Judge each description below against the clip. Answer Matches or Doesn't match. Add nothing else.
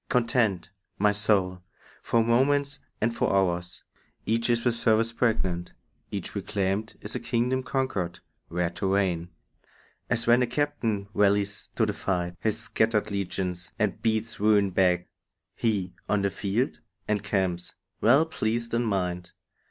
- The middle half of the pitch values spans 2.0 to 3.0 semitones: Doesn't match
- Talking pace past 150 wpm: Doesn't match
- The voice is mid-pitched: Doesn't match